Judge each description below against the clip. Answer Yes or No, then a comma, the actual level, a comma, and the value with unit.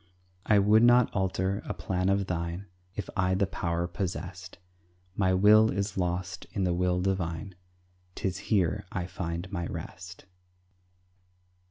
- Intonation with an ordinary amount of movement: No, narrow, 2.0 semitones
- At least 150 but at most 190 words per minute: No, average, 140 wpm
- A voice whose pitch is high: No, very low, 95 Hz